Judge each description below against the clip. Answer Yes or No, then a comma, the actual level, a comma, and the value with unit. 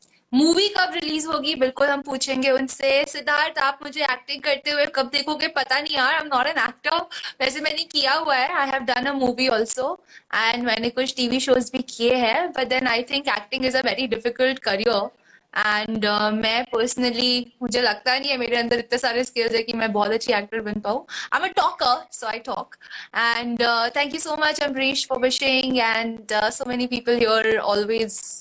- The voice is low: No, very high, 255 Hz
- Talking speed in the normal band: No, fast, 195 wpm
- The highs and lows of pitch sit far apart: No, average, 3.1 semitones